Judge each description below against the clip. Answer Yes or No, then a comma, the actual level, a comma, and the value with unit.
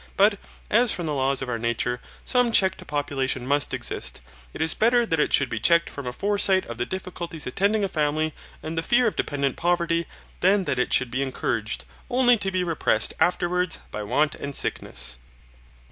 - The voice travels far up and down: Yes, wide, 6.2 semitones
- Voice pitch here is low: No, medium, 160 Hz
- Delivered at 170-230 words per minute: Yes, average, 195 wpm